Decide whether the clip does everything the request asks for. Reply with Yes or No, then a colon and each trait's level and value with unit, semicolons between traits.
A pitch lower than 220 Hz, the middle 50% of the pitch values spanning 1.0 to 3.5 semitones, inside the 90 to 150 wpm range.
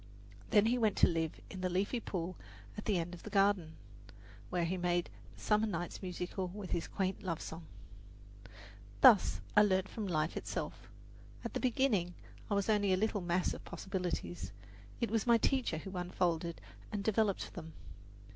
No: medium, 185 Hz; average, 3.0 semitones; average, 175 wpm